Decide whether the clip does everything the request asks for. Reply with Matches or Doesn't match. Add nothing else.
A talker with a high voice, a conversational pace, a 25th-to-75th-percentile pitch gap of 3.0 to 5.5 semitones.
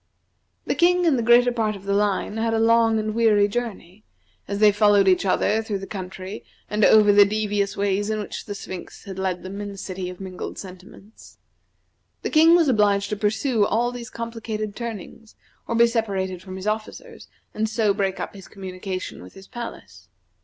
Doesn't match